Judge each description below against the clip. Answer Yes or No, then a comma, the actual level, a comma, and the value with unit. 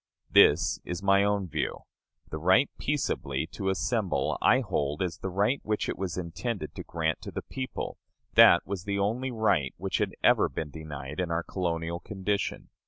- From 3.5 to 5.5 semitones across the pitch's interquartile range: Yes, average, 3.8 semitones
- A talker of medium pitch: No, very low, 95 Hz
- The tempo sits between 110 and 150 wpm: No, average, 175 wpm